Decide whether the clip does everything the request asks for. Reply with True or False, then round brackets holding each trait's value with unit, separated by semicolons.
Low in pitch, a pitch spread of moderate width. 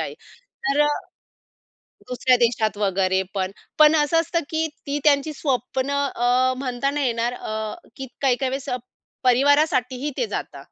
False (260 Hz; 3.0 semitones)